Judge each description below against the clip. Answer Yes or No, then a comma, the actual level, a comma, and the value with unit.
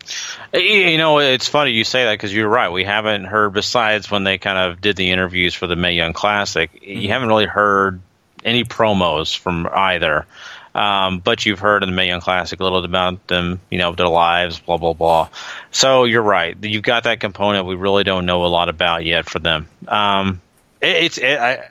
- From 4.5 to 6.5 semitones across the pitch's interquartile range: No, average, 3.2 semitones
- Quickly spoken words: Yes, fast, 215 wpm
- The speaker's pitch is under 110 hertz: Yes, very low, 95 Hz